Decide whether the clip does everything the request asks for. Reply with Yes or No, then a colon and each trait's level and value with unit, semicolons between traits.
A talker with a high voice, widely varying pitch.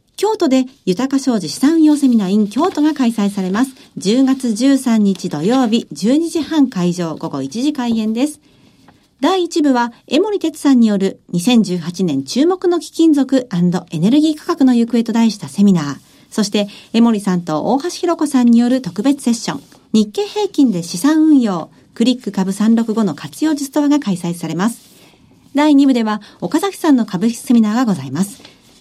Yes: high, 240 Hz; wide, 6.4 semitones